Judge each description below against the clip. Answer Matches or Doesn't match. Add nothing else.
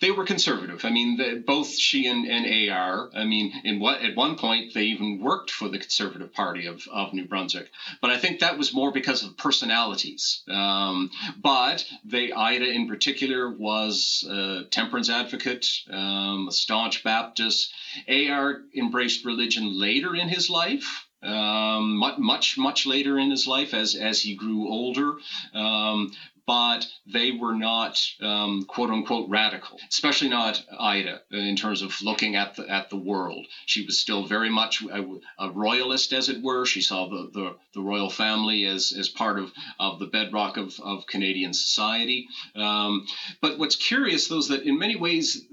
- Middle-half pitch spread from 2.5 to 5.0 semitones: Matches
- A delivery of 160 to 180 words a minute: Matches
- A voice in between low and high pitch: Doesn't match